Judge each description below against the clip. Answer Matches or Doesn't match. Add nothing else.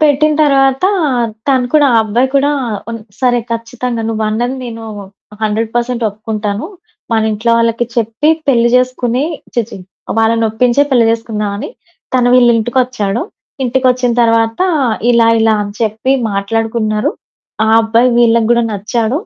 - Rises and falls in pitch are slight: Matches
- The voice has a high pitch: Matches